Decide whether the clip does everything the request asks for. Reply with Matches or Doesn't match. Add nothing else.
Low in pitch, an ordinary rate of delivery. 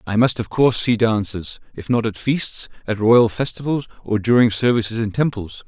Matches